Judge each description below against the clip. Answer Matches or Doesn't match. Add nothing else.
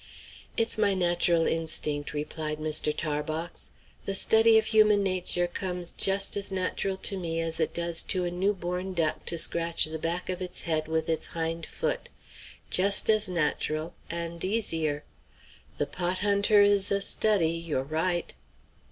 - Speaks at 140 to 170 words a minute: Matches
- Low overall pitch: Doesn't match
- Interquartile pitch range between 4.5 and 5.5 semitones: Doesn't match